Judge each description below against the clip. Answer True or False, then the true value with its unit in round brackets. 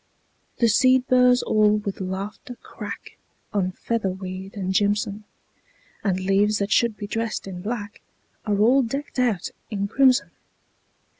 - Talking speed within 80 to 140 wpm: True (135 wpm)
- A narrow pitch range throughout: False (3.4 semitones)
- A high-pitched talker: True (210 Hz)